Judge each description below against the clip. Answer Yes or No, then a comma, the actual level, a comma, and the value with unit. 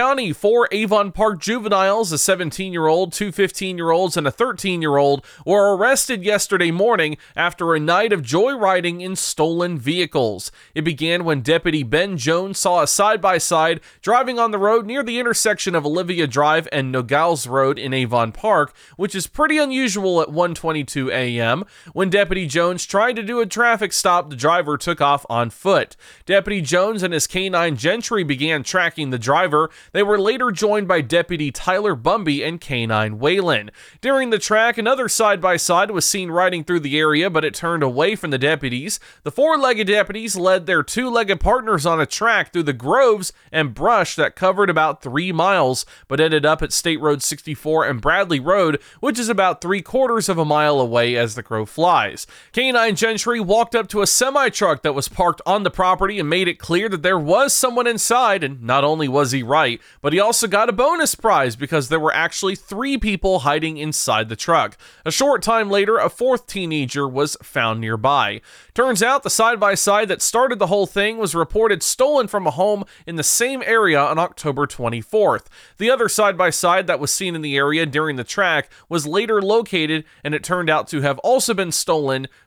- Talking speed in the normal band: Yes, average, 190 wpm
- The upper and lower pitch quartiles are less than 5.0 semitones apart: No, wide, 5.4 semitones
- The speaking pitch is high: No, medium, 180 Hz